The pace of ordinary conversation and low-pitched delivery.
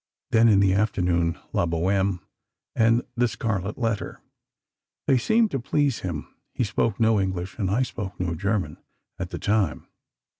Yes: average, 155 wpm; low, 100 Hz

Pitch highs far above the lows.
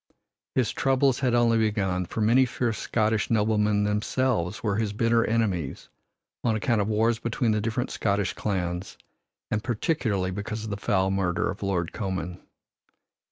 No: average, 2.8 semitones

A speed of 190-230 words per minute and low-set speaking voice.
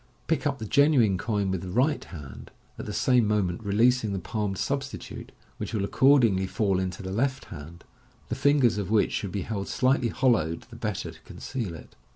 Yes: average, 195 wpm; low, 105 Hz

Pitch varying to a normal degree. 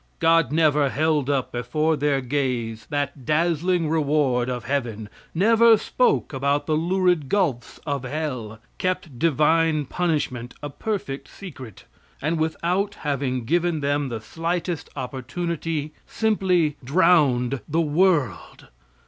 Yes: average, 4.0 semitones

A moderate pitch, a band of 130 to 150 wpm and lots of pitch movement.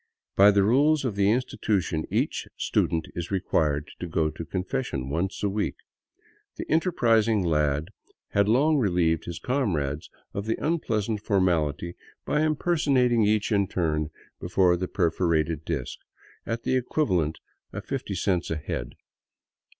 No: very low, 95 Hz; average, 140 wpm; wide, 6.0 semitones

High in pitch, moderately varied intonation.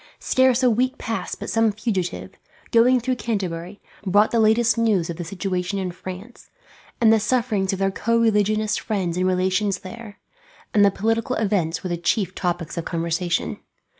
Yes: high, 205 Hz; average, 3.8 semitones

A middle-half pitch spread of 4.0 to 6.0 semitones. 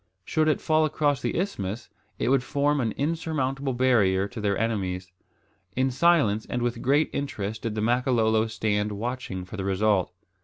Yes: average, 5.1 semitones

